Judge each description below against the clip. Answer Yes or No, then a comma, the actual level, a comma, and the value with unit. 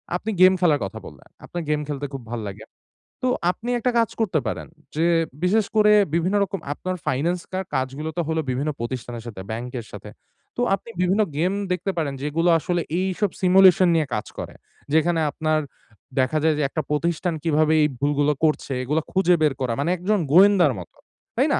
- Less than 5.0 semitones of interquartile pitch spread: Yes, average, 4.4 semitones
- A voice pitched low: No, medium, 160 Hz